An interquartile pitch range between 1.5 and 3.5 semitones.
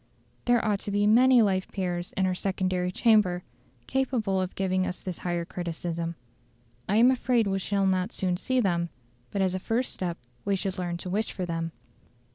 Yes: average, 2.9 semitones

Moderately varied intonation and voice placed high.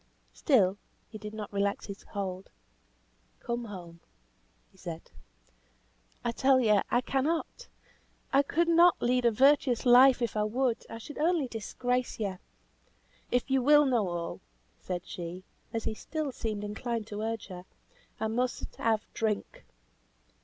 Yes: average, 4.2 semitones; high, 230 Hz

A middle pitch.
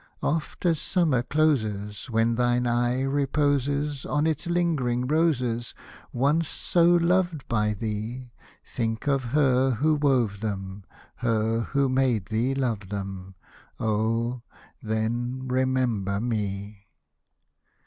No: low, 125 Hz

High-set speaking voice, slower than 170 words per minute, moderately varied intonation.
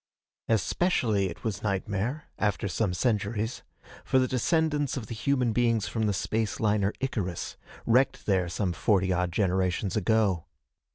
No: low, 105 Hz; average, 145 wpm; average, 3.8 semitones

